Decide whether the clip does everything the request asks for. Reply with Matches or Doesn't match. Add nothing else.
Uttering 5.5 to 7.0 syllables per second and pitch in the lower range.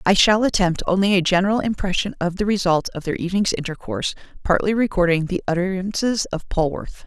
Doesn't match